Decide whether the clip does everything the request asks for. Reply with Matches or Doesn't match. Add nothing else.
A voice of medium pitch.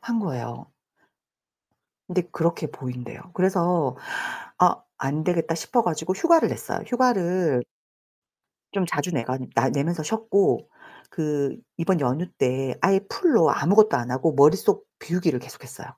Matches